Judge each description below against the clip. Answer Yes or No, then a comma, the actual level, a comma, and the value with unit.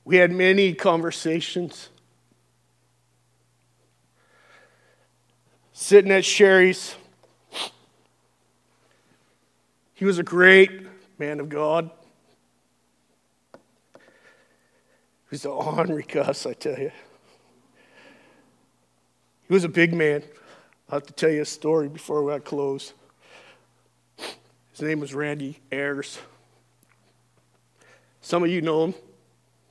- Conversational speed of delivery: No, slow, 95 wpm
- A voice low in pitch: No, medium, 150 Hz